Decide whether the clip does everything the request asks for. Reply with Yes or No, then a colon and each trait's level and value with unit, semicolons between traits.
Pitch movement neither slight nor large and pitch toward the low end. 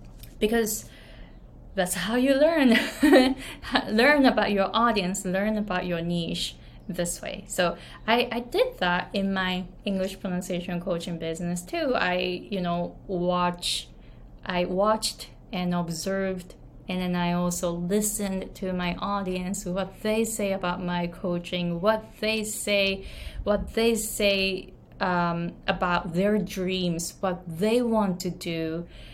No: average, 3.2 semitones; medium, 185 Hz